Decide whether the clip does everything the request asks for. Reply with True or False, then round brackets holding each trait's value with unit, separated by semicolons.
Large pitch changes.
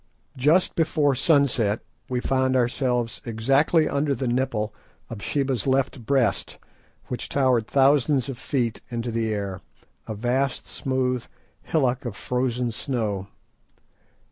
False (2.8 semitones)